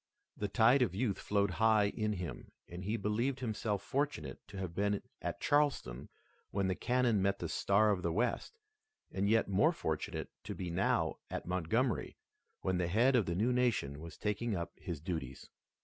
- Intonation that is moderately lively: Yes, average, 4.4 semitones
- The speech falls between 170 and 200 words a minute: Yes, average, 180 wpm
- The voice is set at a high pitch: No, low, 100 Hz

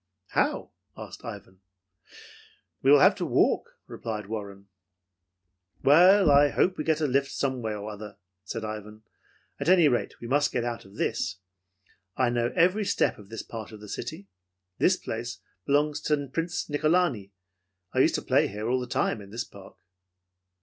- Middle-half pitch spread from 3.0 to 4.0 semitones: No, wide, 5.6 semitones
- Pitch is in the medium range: No, low, 120 Hz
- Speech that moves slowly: No, average, 170 wpm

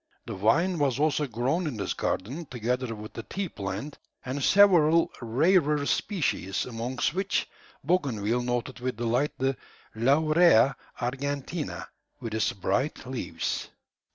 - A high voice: No, low, 130 Hz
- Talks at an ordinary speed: No, slow, 125 wpm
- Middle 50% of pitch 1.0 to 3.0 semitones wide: No, average, 4.8 semitones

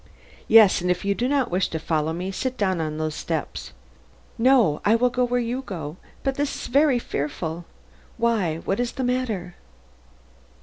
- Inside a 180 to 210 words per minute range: Yes, average, 185 wpm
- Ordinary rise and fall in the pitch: No, wide, 7.1 semitones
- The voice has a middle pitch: No, high, 200 Hz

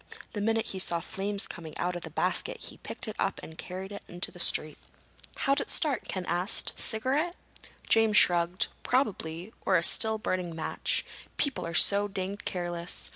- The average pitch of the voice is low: No, high, 190 Hz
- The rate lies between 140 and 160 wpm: No, average, 180 wpm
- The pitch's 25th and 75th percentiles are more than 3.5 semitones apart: Yes, average, 4.0 semitones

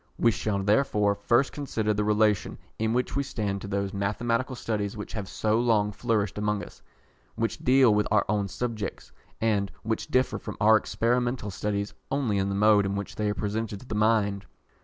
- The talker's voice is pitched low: Yes, low, 105 Hz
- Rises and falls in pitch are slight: Yes, narrow, 2.1 semitones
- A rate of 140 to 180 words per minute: No, average, 190 wpm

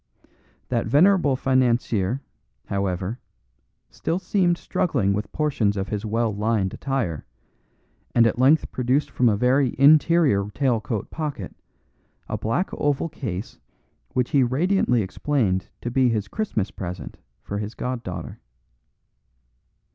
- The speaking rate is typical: No, slow, 125 wpm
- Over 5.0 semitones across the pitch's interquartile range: Yes, wide, 5.6 semitones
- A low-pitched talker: Yes, low, 120 Hz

